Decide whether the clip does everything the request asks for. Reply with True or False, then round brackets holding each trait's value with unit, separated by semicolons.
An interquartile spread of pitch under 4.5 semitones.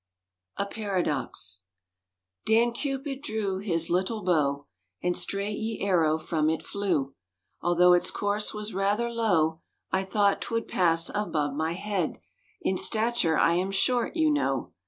False (4.8 semitones)